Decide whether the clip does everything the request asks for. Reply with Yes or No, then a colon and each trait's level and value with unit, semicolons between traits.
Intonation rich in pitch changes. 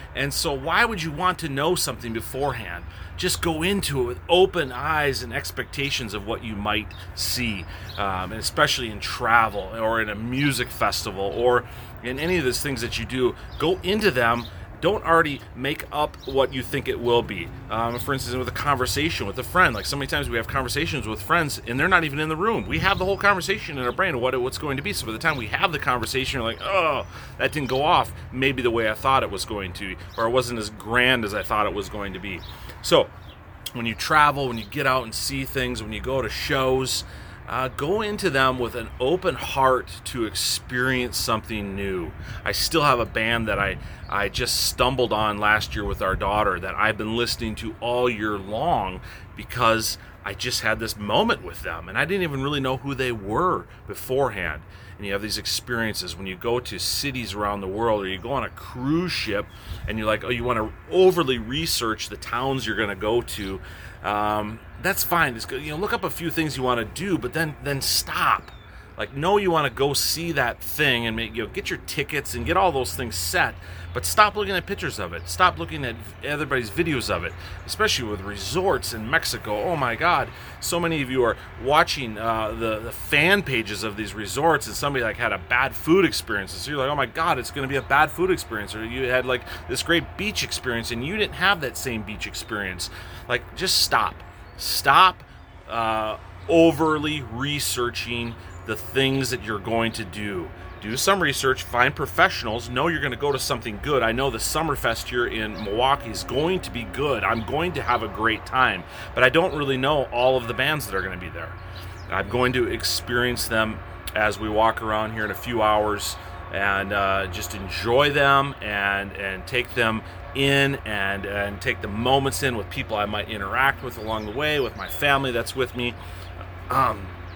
No: average, 4.7 semitones